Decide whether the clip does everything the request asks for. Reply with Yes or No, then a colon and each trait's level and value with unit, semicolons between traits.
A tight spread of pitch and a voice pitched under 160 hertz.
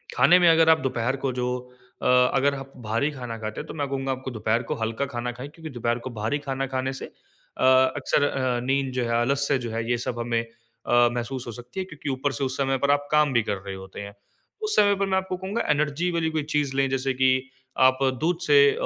No: average, 3.3 semitones; low, 135 Hz